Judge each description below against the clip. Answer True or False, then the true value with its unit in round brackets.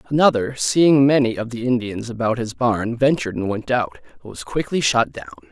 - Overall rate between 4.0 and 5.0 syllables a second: False (5.3 syllables/s)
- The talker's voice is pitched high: False (125 Hz)